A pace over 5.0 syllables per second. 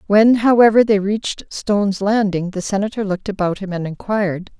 Yes: 5.5 syllables/s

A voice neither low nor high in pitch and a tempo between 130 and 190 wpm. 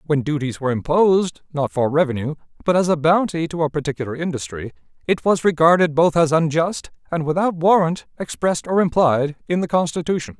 Yes: medium, 160 Hz; average, 175 wpm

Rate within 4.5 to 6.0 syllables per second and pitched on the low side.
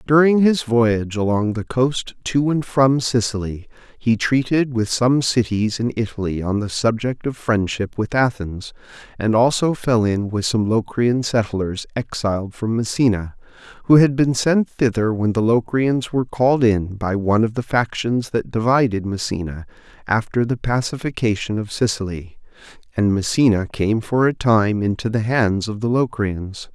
Yes: 4.6 syllables/s; low, 115 Hz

